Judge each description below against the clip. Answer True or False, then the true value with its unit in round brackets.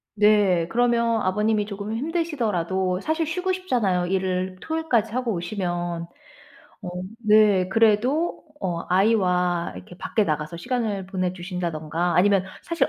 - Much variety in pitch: False (4.4 semitones)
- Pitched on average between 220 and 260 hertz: False (200 Hz)